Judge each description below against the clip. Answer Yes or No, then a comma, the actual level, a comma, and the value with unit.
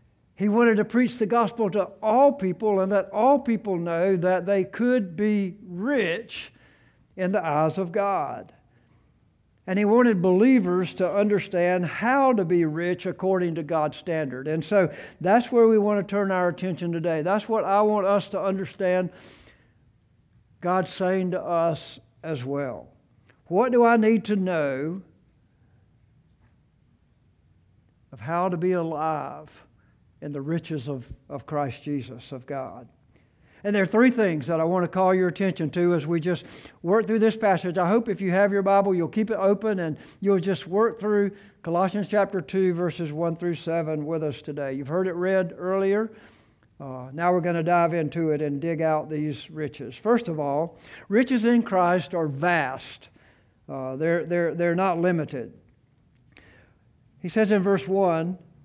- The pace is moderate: Yes, average, 170 wpm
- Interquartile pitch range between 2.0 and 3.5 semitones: No, average, 4.1 semitones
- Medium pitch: Yes, medium, 180 Hz